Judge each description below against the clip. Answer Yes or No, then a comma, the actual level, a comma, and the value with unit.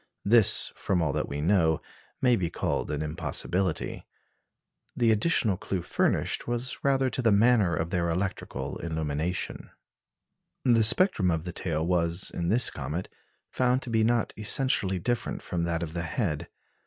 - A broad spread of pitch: Yes, wide, 5.8 semitones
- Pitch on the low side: Yes, very low, 95 Hz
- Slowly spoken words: No, average, 155 wpm